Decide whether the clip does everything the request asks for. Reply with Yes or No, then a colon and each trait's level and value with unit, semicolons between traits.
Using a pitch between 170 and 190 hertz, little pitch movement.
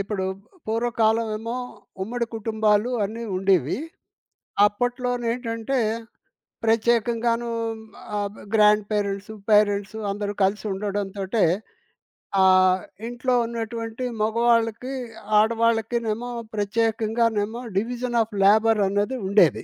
No: high, 220 Hz; narrow, 2.3 semitones